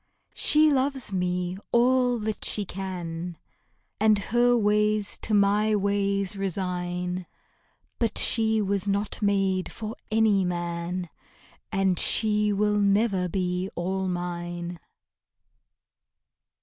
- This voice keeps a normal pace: No, slow, 105 wpm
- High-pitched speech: Yes, high, 200 Hz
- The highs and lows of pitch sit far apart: No, average, 2.9 semitones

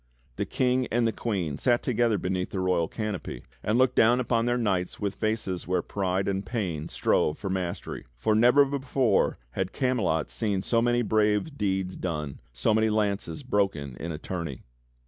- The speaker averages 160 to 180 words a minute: Yes, average, 175 wpm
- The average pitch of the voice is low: Yes, low, 105 Hz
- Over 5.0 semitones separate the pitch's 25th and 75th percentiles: No, average, 4.5 semitones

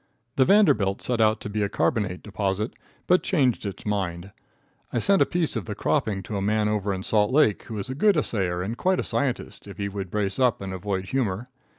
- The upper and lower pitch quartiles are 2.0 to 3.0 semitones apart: No, average, 4.6 semitones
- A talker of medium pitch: No, low, 105 Hz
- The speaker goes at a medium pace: No, fast, 225 wpm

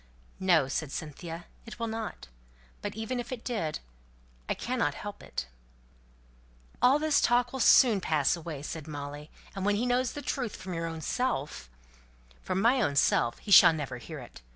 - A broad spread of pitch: Yes, wide, 8.3 semitones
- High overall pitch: No, medium, 175 Hz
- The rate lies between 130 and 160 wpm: No, average, 180 wpm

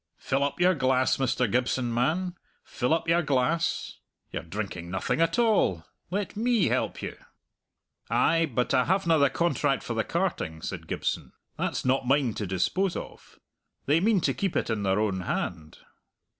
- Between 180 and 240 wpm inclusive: No, average, 170 wpm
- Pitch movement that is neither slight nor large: No, wide, 7.3 semitones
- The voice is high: No, low, 135 Hz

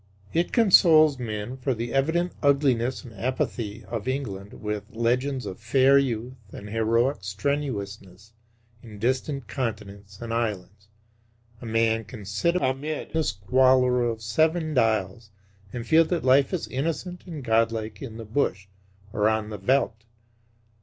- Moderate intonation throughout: Yes, average, 4.2 semitones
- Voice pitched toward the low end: Yes, low, 120 Hz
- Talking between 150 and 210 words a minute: No, average, 140 wpm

